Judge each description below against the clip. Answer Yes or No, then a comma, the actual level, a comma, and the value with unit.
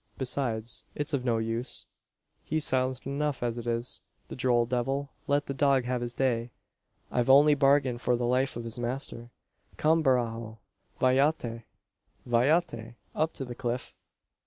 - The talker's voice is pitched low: Yes, low, 125 Hz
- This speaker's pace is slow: No, average, 155 wpm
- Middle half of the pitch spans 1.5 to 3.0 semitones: Yes, narrow, 2.6 semitones